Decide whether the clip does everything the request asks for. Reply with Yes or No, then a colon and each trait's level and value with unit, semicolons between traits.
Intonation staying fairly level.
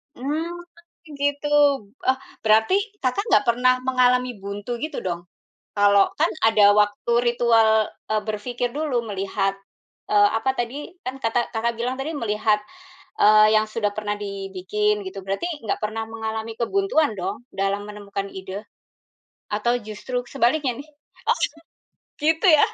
No: average, 3.6 semitones